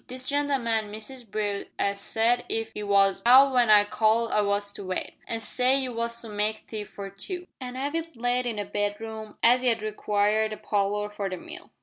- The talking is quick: Yes, fast, 210 wpm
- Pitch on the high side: Yes, high, 220 Hz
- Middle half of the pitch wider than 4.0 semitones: No, average, 3.1 semitones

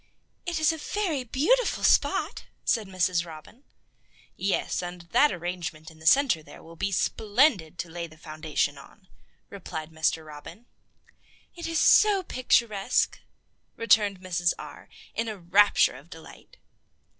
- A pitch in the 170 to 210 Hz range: Yes, medium, 185 Hz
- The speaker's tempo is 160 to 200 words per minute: No, average, 140 wpm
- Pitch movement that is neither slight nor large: No, wide, 7.0 semitones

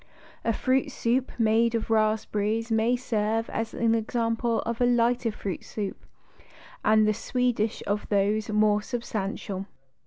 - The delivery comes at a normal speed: No, slow, 130 wpm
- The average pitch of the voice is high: Yes, high, 225 Hz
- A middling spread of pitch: No, narrow, 1.6 semitones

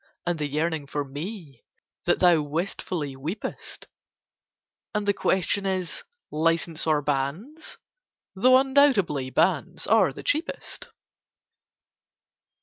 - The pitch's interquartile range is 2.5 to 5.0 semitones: No, wide, 5.4 semitones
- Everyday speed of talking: No, slow, 105 wpm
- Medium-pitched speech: Yes, medium, 170 Hz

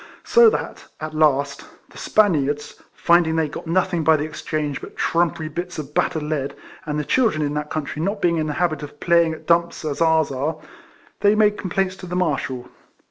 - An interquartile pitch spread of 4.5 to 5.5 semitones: No, average, 2.7 semitones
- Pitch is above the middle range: No, medium, 160 Hz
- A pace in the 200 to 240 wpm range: Yes, fast, 205 wpm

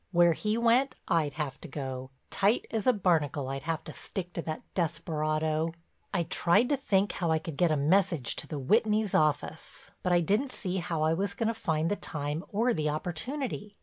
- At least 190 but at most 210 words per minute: Yes, fast, 205 wpm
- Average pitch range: Yes, average, 5.0 semitones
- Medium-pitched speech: Yes, medium, 170 Hz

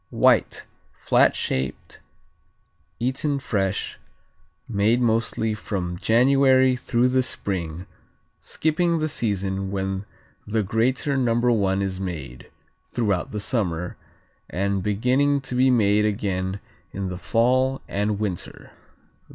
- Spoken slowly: Yes, slow, 110 wpm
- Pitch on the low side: Yes, low, 105 Hz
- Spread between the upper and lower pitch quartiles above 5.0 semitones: No, average, 4.7 semitones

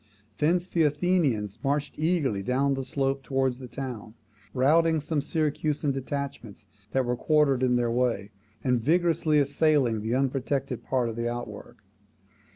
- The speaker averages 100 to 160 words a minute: Yes, average, 145 wpm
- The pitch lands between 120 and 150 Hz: Yes, low, 135 Hz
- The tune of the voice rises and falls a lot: No, average, 3.6 semitones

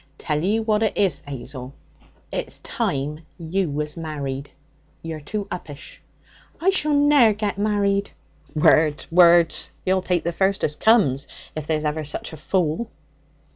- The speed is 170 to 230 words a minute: No, average, 145 wpm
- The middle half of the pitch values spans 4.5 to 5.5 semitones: Yes, average, 5.2 semitones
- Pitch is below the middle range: No, medium, 170 Hz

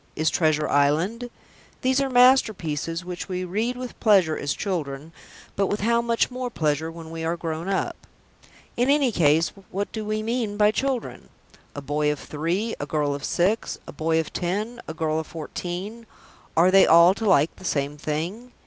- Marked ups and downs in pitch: Yes, wide, 6.0 semitones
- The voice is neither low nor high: Yes, medium, 180 Hz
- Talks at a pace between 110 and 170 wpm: No, average, 185 wpm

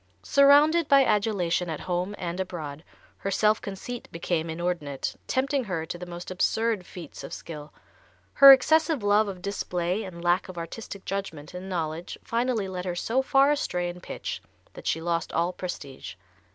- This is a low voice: No, medium, 185 Hz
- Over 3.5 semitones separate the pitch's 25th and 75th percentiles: Yes, average, 4.6 semitones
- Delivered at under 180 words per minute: Yes, average, 165 wpm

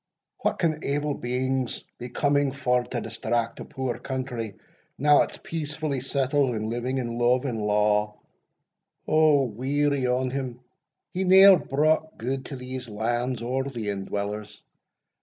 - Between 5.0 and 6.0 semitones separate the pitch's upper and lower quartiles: No, average, 3.2 semitones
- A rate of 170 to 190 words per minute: No, average, 140 wpm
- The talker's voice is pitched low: Yes, low, 130 Hz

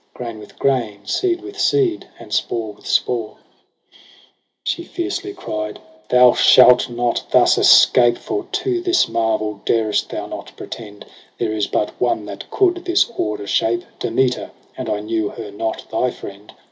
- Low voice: Yes, low, 115 Hz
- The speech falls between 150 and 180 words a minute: Yes, average, 170 wpm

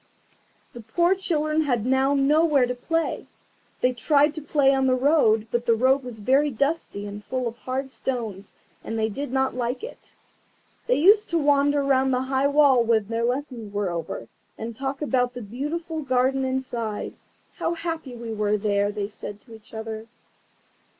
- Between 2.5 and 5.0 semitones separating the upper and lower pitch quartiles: Yes, average, 4.2 semitones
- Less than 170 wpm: No, average, 175 wpm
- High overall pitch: Yes, very high, 260 Hz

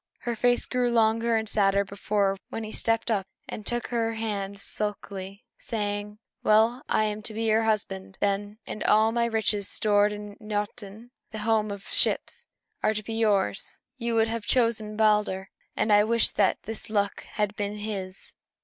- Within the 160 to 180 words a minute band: Yes, average, 175 wpm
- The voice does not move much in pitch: Yes, narrow, 1.7 semitones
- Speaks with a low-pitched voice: No, high, 215 Hz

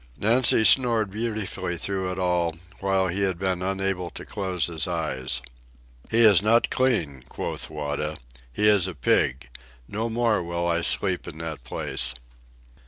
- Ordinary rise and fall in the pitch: Yes, average, 4.2 semitones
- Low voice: Yes, very low, 95 Hz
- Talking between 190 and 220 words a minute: No, average, 155 wpm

